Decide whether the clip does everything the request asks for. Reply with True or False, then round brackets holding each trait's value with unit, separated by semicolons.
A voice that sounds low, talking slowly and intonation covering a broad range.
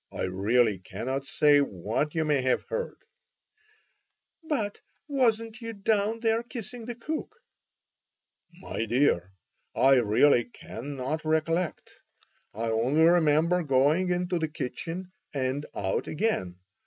False (155 Hz; 115 wpm; 8.1 semitones)